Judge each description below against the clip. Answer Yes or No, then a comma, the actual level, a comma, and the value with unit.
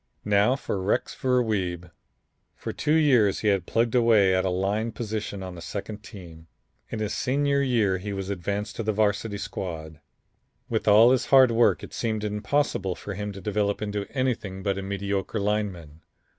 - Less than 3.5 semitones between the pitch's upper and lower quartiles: Yes, average, 2.9 semitones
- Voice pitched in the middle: No, low, 105 Hz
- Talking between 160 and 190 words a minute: Yes, average, 180 wpm